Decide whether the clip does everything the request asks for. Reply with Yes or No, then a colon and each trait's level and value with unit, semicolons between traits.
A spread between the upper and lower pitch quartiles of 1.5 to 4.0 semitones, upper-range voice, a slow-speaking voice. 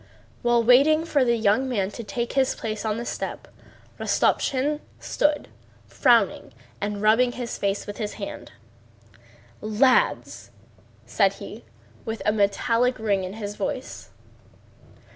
Yes: average, 3.5 semitones; high, 230 Hz; slow, 130 wpm